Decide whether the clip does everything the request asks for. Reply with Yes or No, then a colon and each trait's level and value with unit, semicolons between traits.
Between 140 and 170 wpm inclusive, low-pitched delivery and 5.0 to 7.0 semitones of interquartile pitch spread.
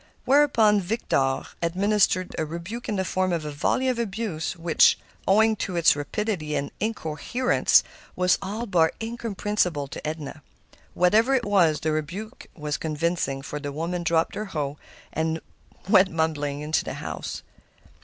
No: average, 150 wpm; medium, 175 Hz; wide, 5.4 semitones